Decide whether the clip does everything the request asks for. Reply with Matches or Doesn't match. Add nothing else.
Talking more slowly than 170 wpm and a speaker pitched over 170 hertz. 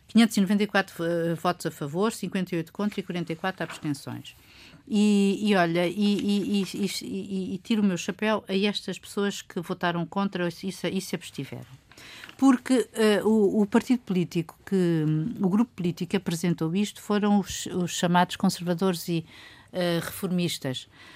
Matches